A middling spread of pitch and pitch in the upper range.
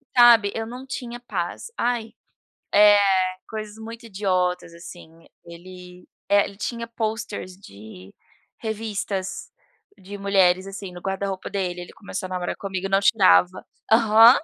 Yes: average, 3.4 semitones; high, 200 Hz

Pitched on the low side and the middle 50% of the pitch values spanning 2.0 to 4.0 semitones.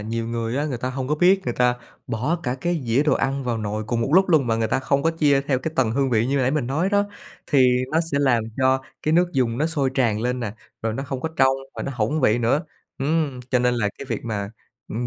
Yes: low, 130 Hz; average, 3.7 semitones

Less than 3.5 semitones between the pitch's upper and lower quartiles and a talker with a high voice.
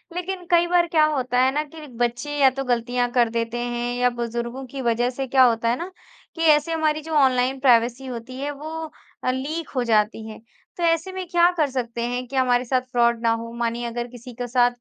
No: average, 3.8 semitones; very high, 250 Hz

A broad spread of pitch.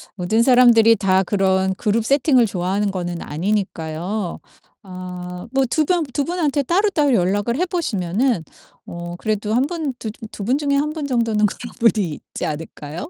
Yes: wide, 6.5 semitones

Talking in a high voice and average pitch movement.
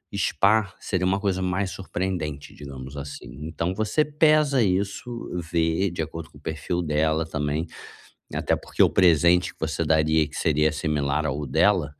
No: very low, 85 Hz; average, 4.0 semitones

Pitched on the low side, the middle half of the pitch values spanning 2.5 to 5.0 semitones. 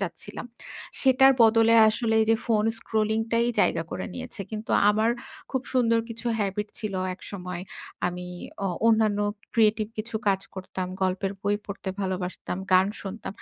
No: high, 215 Hz; average, 2.9 semitones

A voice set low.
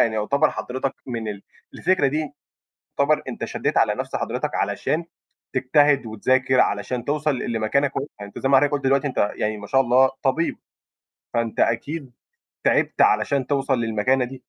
Yes: low, 130 Hz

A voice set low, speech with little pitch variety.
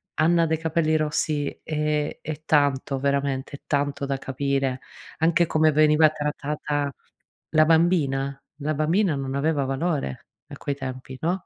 No: medium, 150 Hz; narrow, 2.2 semitones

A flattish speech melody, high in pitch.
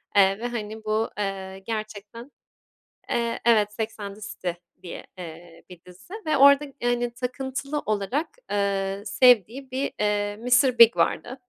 No: average, 3.7 semitones; high, 215 Hz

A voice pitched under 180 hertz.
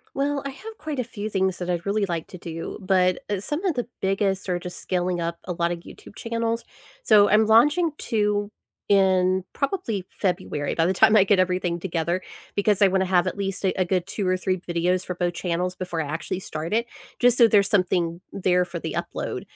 No: high, 190 Hz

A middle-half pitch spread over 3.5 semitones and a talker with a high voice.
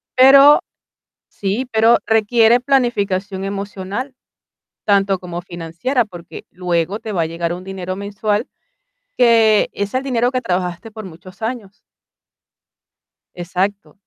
Yes: average, 3.9 semitones; high, 200 Hz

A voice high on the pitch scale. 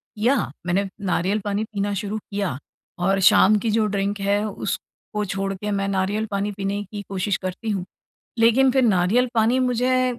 Yes: high, 205 Hz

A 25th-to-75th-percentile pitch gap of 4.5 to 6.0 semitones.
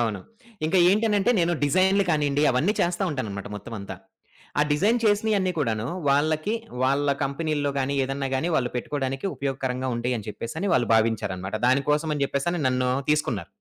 Yes: average, 5.1 semitones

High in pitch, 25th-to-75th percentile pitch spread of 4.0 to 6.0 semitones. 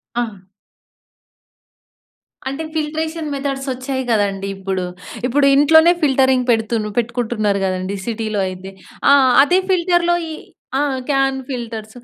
Yes: very high, 255 Hz; average, 5.3 semitones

